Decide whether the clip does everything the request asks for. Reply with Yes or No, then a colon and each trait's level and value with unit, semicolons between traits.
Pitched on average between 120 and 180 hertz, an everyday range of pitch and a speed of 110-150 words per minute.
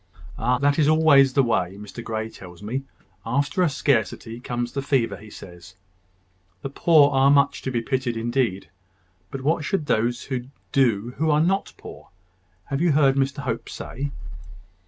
No: low, 135 Hz; average, 3.8 semitones; average, 165 wpm